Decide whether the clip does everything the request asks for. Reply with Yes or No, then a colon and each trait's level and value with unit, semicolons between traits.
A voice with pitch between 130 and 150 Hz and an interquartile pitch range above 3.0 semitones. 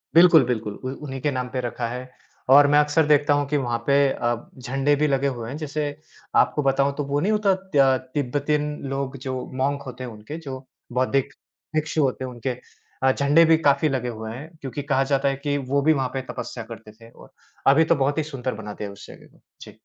No: low, 135 Hz; average, 2.7 semitones